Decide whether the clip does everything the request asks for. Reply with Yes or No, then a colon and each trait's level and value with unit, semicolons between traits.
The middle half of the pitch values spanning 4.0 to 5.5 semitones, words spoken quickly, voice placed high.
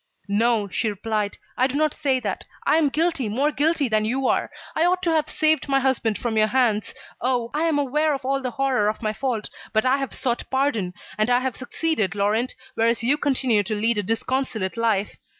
Yes: average, 4.3 semitones; fast, 215 wpm; very high, 250 Hz